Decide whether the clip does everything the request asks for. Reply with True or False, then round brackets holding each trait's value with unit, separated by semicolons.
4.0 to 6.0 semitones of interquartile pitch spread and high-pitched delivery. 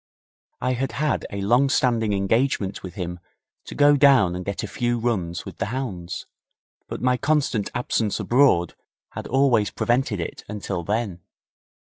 False (5.1 semitones; 115 Hz)